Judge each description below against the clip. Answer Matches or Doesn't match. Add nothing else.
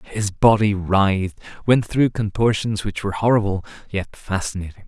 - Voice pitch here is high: Doesn't match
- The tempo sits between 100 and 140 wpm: Matches